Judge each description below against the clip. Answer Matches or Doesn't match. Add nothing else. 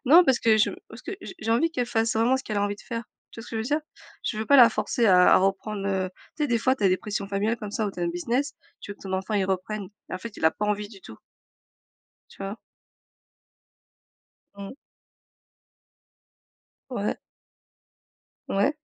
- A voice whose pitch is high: Matches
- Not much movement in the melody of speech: Doesn't match